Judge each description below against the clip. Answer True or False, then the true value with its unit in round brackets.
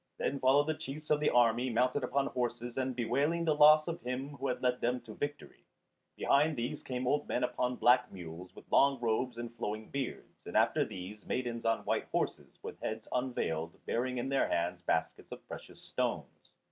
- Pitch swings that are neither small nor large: True (3.0 semitones)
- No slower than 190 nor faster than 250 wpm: True (195 wpm)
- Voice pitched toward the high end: False (125 Hz)